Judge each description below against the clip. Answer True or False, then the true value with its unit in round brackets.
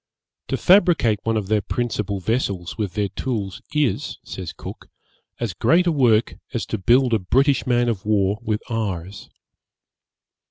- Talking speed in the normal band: True (155 wpm)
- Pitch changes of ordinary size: True (3.8 semitones)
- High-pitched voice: False (110 Hz)